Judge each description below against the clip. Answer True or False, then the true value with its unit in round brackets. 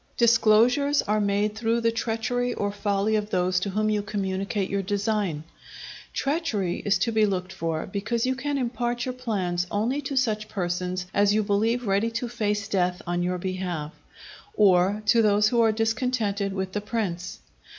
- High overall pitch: True (210 Hz)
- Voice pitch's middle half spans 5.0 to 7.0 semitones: False (3.2 semitones)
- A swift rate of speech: False (170 wpm)